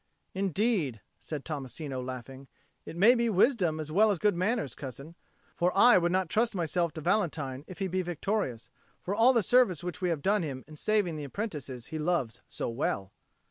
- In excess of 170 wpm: Yes, average, 190 wpm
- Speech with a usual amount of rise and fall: No, wide, 6.2 semitones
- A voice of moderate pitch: Yes, medium, 175 Hz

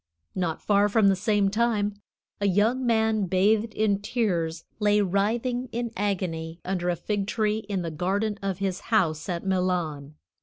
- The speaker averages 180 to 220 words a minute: No, average, 160 wpm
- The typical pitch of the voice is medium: No, high, 200 Hz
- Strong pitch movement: No, average, 3.2 semitones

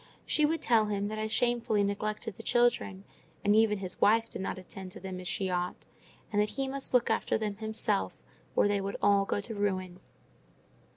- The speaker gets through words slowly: No, fast, 205 wpm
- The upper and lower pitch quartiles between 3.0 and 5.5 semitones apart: No, narrow, 2.4 semitones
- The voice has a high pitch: Yes, high, 205 Hz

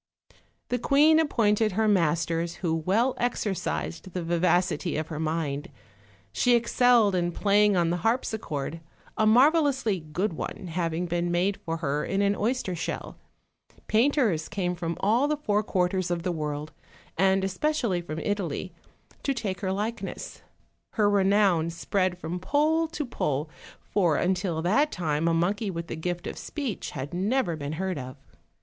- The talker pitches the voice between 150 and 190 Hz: Yes, medium, 185 Hz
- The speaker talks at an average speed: Yes, average, 155 wpm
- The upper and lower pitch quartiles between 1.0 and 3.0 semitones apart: No, average, 4.6 semitones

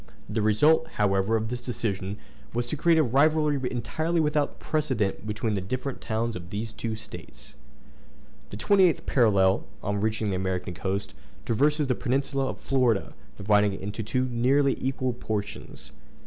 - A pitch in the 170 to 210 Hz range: No, low, 115 Hz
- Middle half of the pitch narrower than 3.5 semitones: No, average, 4.9 semitones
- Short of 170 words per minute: Yes, average, 155 wpm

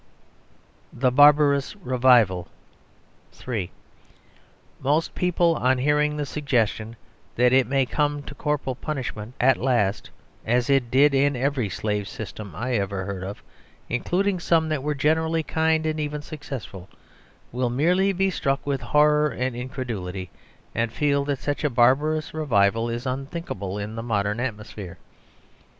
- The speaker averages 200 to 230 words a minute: No, average, 140 wpm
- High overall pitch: No, low, 130 Hz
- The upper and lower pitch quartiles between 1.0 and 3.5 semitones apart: No, average, 4.6 semitones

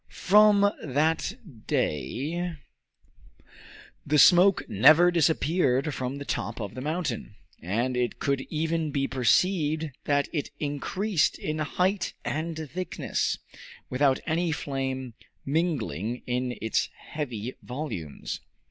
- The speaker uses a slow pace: Yes, slow, 110 wpm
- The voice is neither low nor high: Yes, medium, 150 Hz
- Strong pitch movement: No, average, 4.6 semitones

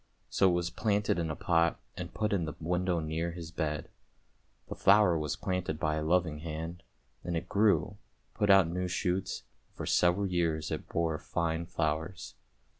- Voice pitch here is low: Yes, very low, 85 Hz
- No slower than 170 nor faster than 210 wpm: Yes, average, 180 wpm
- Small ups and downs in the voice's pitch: Yes, narrow, 2.3 semitones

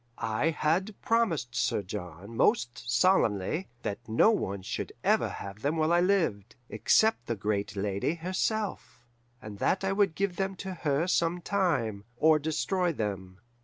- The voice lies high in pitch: No, medium, 155 Hz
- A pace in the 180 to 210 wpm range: No, average, 155 wpm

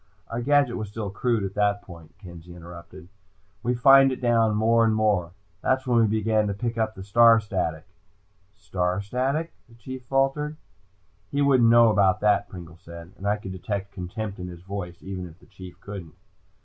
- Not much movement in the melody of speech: No, average, 4.2 semitones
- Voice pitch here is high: No, low, 105 Hz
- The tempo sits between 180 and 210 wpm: Yes, average, 190 wpm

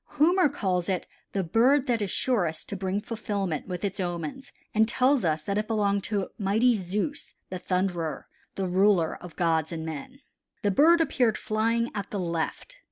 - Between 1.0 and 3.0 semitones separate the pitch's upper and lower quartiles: No, average, 4.6 semitones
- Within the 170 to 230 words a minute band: Yes, average, 175 wpm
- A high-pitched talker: Yes, high, 200 Hz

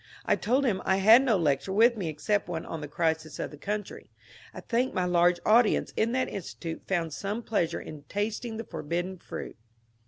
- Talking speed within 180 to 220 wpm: Yes, average, 195 wpm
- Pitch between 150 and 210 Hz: Yes, high, 190 Hz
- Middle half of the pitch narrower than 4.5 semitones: No, average, 5.1 semitones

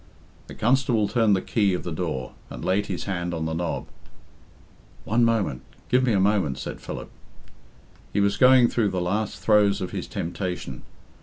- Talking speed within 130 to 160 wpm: No, average, 175 wpm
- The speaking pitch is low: Yes, low, 100 Hz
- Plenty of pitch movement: No, average, 4.0 semitones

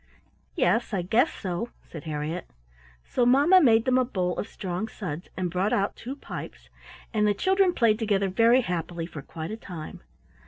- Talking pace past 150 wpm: Yes, average, 180 wpm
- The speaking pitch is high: Yes, high, 205 Hz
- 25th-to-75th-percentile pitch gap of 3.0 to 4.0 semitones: No, average, 5.3 semitones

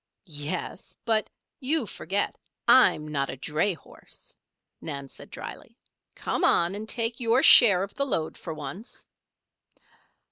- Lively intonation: Yes, wide, 6.9 semitones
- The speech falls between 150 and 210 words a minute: No, slow, 135 wpm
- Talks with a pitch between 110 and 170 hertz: No, high, 190 Hz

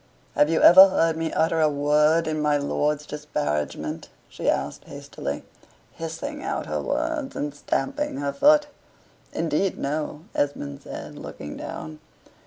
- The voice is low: No, medium, 150 Hz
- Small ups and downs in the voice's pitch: Yes, narrow, 2.3 semitones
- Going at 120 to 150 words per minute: Yes, average, 140 wpm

